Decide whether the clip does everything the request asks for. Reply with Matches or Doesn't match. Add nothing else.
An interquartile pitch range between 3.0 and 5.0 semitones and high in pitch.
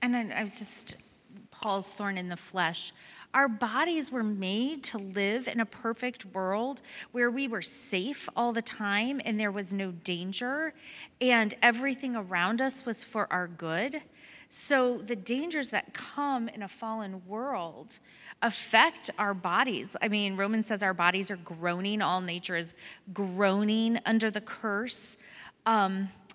Matches